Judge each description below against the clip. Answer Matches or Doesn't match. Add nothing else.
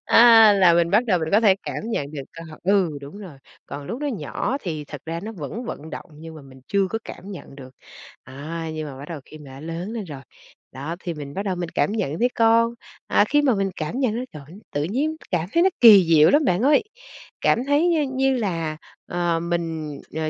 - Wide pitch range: Matches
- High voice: Doesn't match